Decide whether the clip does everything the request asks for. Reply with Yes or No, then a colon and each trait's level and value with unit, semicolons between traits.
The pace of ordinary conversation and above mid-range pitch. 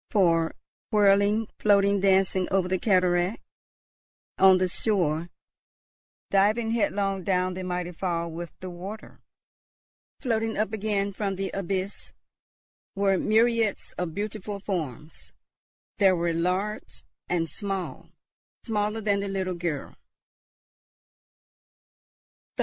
No: slow, 105 wpm; high, 195 Hz